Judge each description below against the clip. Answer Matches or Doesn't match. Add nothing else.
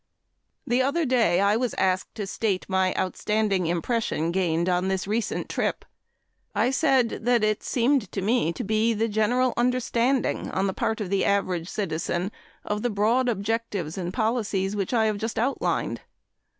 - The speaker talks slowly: Doesn't match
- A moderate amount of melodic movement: Matches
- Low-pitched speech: Doesn't match